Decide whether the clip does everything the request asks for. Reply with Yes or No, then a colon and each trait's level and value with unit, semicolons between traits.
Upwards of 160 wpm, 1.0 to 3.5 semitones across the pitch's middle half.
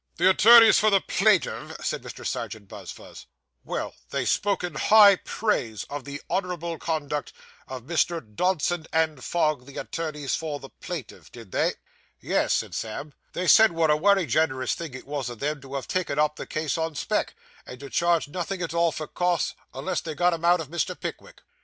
No: average, 190 wpm; average, 4.0 semitones